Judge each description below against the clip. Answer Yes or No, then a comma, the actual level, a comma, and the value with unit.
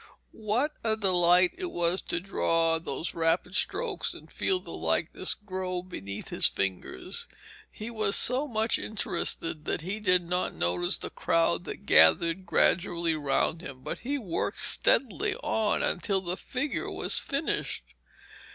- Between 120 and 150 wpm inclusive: Yes, average, 145 wpm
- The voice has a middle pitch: Yes, medium, 180 Hz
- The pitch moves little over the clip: No, average, 4.8 semitones